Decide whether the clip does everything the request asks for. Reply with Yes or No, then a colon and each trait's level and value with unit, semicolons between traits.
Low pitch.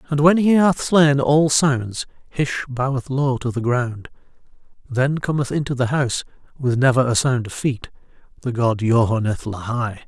Yes: low, 130 Hz